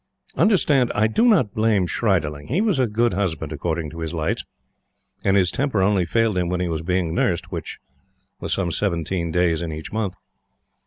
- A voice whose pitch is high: No, very low, 90 Hz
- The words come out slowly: No, average, 190 wpm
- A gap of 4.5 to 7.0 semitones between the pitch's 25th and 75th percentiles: Yes, average, 4.9 semitones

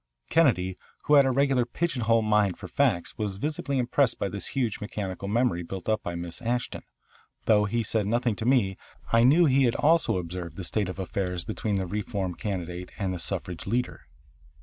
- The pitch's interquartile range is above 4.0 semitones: Yes, average, 4.8 semitones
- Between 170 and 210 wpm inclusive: Yes, average, 195 wpm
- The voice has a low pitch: Yes, low, 105 Hz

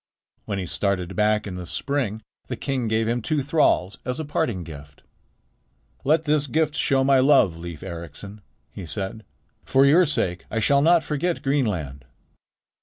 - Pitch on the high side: No, low, 115 Hz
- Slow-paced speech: No, average, 165 wpm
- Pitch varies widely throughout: Yes, wide, 7.5 semitones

